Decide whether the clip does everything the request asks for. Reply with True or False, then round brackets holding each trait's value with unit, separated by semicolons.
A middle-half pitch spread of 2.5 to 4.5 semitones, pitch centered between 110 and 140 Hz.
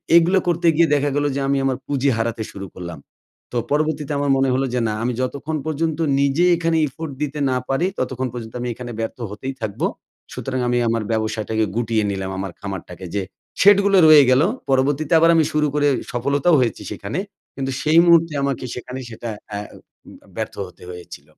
False (5.1 semitones; 135 Hz)